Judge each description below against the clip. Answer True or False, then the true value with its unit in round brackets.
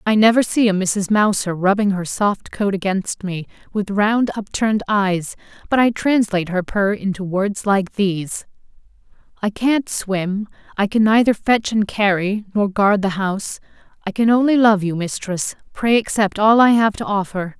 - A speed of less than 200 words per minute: True (170 wpm)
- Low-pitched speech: False (205 Hz)